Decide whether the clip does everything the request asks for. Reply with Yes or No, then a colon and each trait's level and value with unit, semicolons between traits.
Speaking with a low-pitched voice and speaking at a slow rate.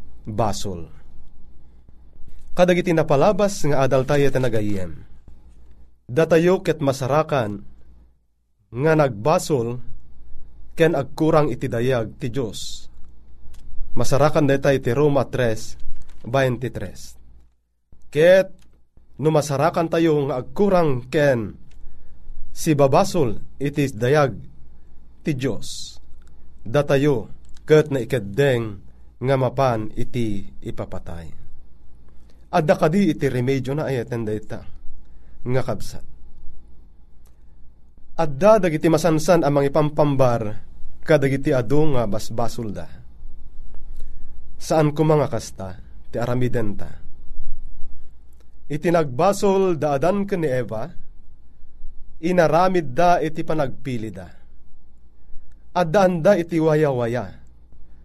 Yes: low, 110 Hz; slow, 90 wpm